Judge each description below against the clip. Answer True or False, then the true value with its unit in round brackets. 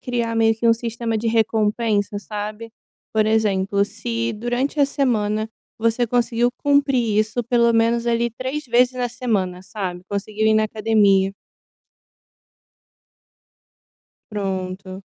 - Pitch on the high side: True (225 Hz)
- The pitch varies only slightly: True (2.3 semitones)